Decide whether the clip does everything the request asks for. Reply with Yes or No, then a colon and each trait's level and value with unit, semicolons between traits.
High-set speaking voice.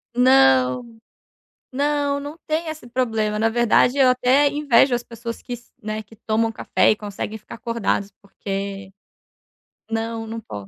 Yes: high, 230 Hz